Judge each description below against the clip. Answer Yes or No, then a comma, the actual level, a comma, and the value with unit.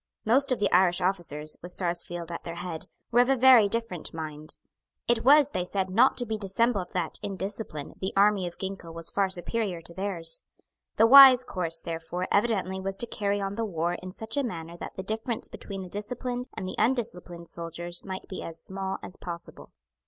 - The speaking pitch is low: No, high, 190 Hz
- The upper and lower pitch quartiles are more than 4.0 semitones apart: Yes, average, 4.5 semitones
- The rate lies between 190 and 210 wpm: Yes, average, 200 wpm